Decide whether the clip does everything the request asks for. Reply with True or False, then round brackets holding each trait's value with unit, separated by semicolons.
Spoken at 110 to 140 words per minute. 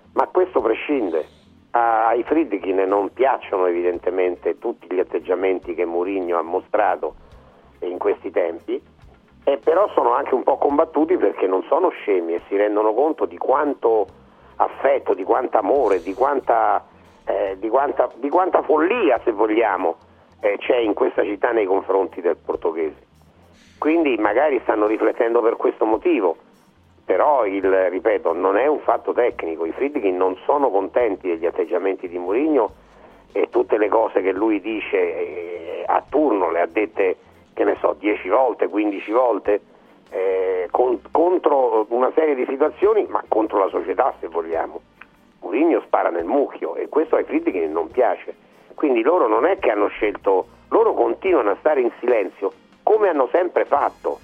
False (155 wpm)